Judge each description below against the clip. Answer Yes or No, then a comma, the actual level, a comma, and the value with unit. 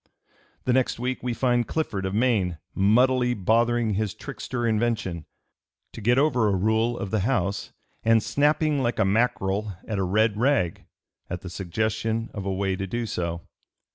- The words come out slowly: No, average, 170 wpm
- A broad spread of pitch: No, average, 4.0 semitones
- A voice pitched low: Yes, low, 110 Hz